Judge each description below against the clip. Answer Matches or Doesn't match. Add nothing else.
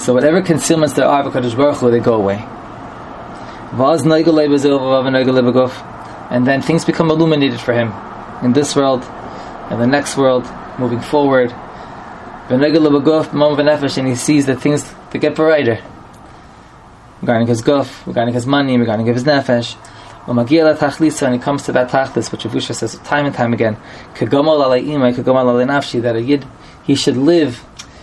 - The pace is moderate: Doesn't match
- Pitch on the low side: Matches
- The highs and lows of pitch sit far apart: Doesn't match